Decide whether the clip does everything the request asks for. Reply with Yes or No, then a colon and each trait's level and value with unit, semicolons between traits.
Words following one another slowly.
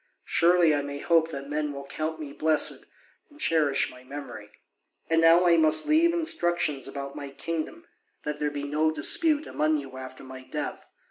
No: average, 185 wpm